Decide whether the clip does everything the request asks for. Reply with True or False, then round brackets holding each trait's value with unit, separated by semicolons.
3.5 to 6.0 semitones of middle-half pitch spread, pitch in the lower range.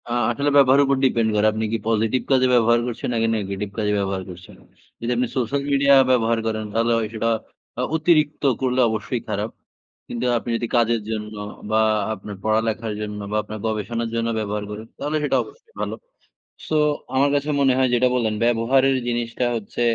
False (3.0 semitones; 115 Hz)